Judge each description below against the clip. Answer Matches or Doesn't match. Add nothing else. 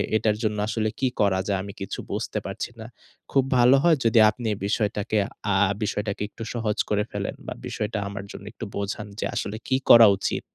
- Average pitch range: Doesn't match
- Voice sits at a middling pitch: Doesn't match